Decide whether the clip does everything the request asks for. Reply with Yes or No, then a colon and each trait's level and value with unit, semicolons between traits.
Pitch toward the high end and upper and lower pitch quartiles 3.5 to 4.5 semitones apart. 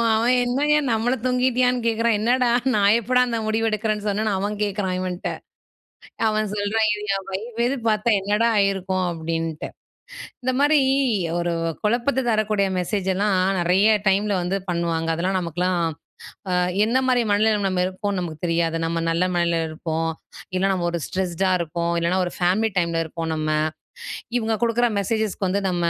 Yes: high, 200 Hz; average, 4.1 semitones